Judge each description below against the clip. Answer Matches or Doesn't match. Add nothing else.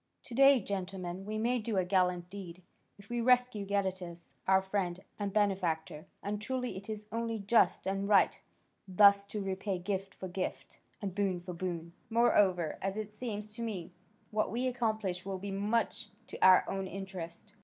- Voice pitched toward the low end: Doesn't match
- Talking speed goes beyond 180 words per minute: Doesn't match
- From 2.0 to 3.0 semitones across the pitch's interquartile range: Matches